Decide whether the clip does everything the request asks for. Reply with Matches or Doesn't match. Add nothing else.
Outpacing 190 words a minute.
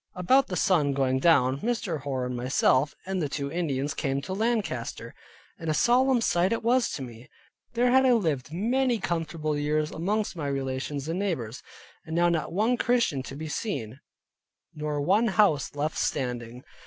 Doesn't match